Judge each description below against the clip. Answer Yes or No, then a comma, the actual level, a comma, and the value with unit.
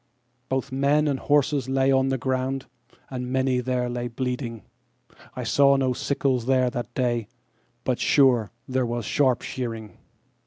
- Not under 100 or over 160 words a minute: Yes, average, 140 wpm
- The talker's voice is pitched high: No, low, 130 Hz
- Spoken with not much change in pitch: Yes, narrow, 1.7 semitones